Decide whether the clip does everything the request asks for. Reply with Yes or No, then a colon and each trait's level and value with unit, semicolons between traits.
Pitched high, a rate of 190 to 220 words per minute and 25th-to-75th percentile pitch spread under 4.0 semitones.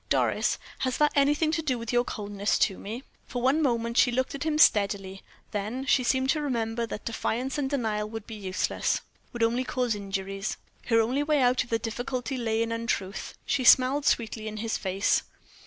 Yes: high, 235 Hz; average, 195 wpm; average, 3.4 semitones